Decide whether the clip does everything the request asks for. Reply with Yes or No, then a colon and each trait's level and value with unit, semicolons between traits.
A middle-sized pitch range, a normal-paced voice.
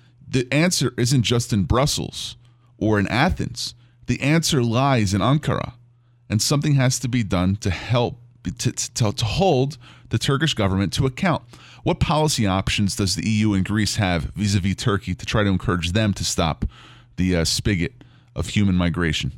Yes: average, 4.3 semitones; average, 175 wpm